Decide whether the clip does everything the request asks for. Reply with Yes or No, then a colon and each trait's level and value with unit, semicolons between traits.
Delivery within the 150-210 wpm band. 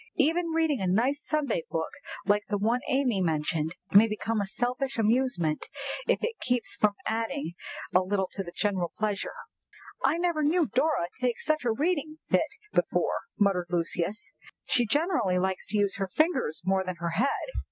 Yes: average, 175 wpm